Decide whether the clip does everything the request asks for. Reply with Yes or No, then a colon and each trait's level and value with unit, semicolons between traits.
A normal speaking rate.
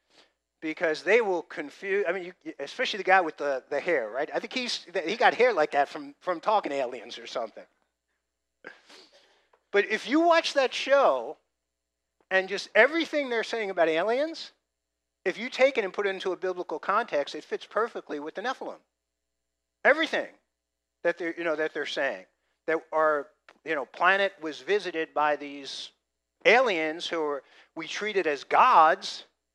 Yes: average, 170 wpm